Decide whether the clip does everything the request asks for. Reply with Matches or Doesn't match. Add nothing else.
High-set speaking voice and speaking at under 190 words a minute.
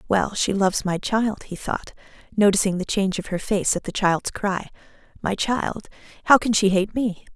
Doesn't match